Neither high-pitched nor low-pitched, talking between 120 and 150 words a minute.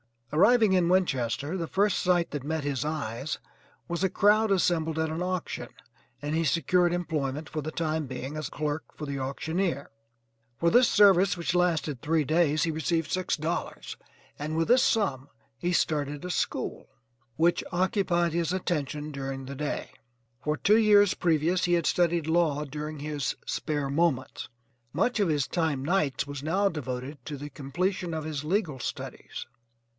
No: medium, 160 Hz; average, 165 wpm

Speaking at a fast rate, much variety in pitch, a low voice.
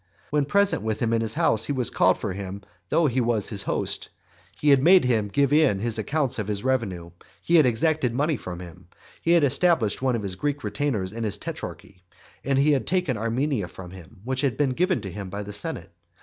Yes: fast, 225 wpm; wide, 6.0 semitones; low, 120 Hz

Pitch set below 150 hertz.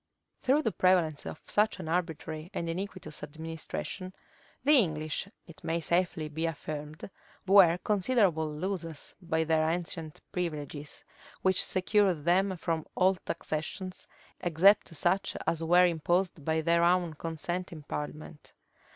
No: medium, 170 Hz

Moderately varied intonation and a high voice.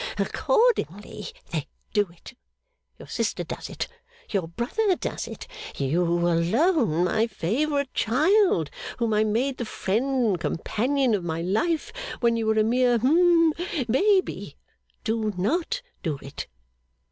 No: wide, 8.6 semitones; high, 230 Hz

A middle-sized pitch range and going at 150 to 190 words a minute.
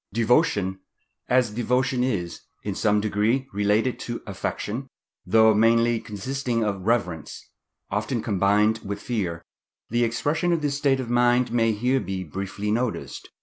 No: average, 3.4 semitones; slow, 135 wpm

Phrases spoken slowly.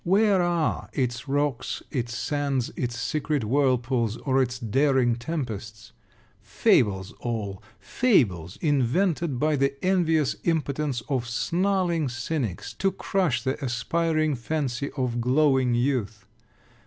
Yes: slow, 115 wpm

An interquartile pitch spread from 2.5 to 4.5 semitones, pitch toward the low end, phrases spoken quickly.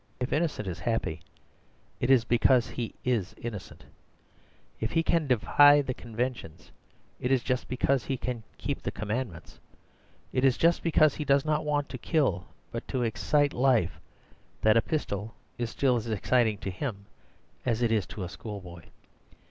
No: average, 4.2 semitones; low, 120 Hz; average, 170 wpm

